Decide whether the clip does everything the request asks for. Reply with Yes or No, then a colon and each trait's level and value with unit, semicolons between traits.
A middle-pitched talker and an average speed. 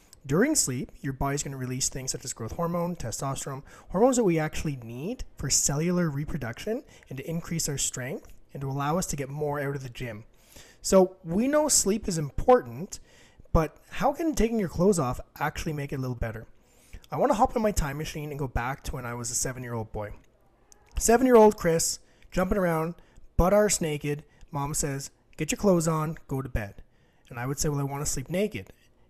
No: medium, 150 Hz; fast, 215 wpm